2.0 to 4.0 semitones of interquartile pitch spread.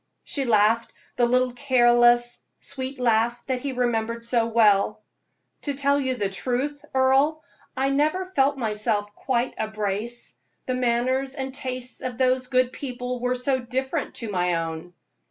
Yes: narrow, 2.4 semitones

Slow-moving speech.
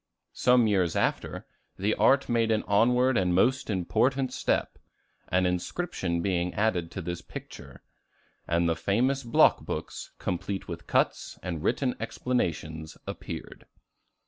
Yes: slow, 130 wpm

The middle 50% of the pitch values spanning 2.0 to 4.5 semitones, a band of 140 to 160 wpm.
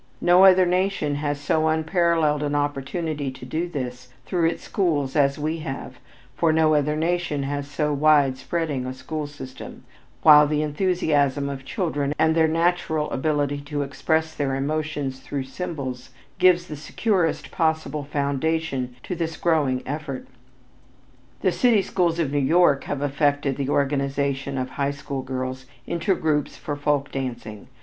Yes: average, 2.7 semitones; average, 155 wpm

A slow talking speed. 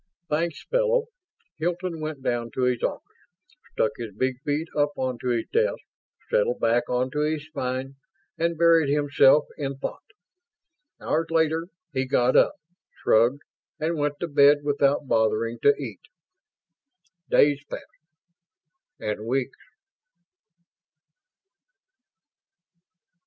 Yes: slow, 115 wpm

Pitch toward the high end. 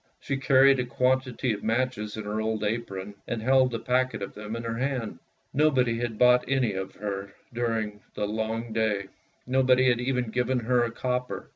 No: low, 120 Hz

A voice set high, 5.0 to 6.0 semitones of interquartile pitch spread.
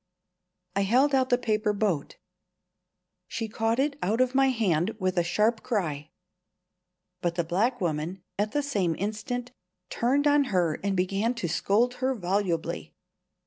Yes: high, 215 Hz; wide, 5.4 semitones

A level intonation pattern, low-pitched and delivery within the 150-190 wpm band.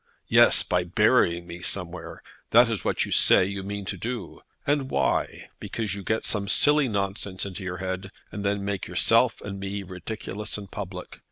Yes: narrow, 2.3 semitones; low, 100 Hz; average, 180 wpm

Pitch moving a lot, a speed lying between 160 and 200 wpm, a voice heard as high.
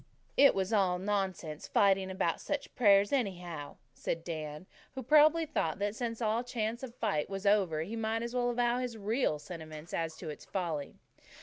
Yes: wide, 5.8 semitones; average, 185 wpm; high, 200 Hz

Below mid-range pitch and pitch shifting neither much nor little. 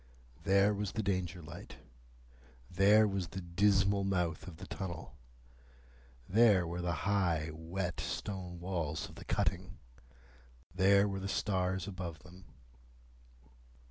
No: very low, 95 Hz; narrow, 2.2 semitones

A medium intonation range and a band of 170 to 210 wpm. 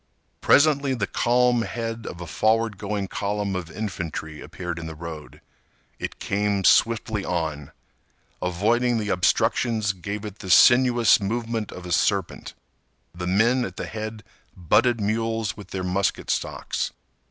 No: average, 4.0 semitones; average, 140 wpm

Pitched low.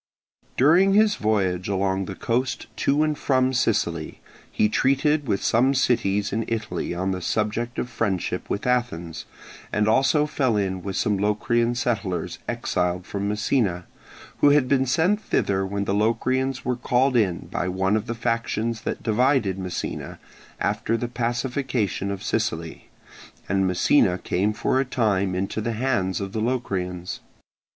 Yes: low, 110 Hz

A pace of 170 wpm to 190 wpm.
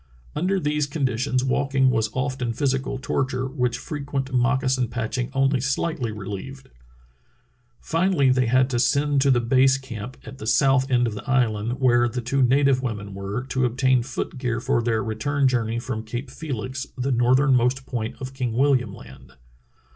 Yes: average, 175 wpm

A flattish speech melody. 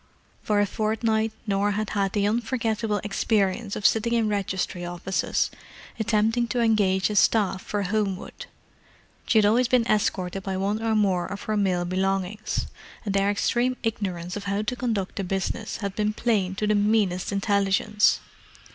Yes: narrow, 2.1 semitones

